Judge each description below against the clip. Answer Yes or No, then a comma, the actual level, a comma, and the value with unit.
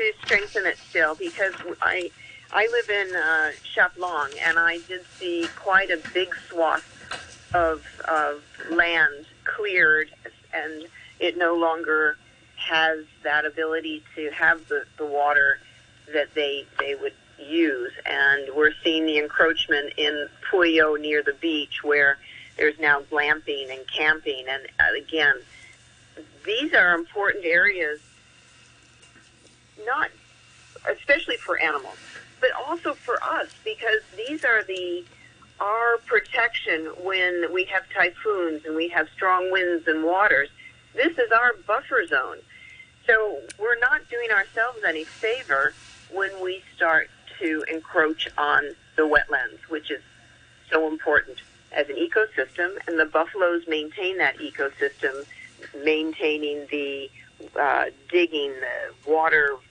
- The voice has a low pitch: No, medium, 170 Hz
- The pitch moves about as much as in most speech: No, wide, 8.4 semitones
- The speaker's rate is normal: No, slow, 125 wpm